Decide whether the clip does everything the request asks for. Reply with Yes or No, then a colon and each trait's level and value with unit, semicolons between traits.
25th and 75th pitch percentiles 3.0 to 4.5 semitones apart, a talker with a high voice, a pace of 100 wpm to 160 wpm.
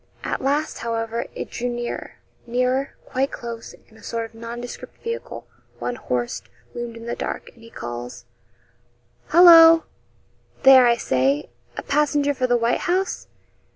Yes: average, 3.3 semitones; high, 240 Hz; average, 150 wpm